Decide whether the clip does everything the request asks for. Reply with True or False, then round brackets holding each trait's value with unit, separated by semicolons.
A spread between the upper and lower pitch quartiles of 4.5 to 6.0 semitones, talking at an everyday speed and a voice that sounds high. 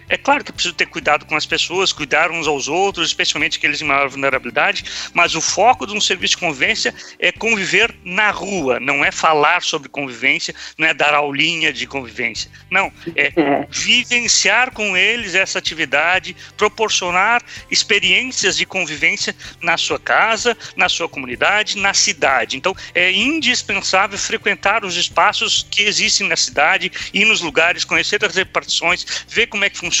False (5.1 semitones; 165 wpm; 180 Hz)